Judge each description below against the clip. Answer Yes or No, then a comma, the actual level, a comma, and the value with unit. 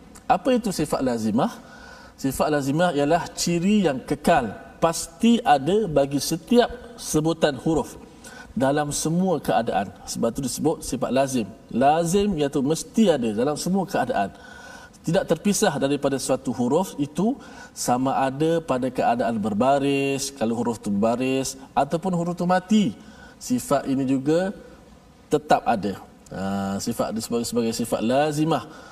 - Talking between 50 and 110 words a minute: No, fast, 125 wpm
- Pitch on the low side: No, medium, 175 Hz